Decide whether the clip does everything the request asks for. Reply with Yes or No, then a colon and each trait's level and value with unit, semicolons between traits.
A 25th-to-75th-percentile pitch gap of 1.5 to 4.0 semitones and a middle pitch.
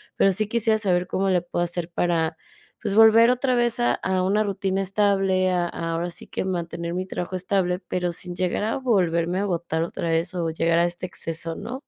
Yes: narrow, 2.6 semitones; medium, 180 Hz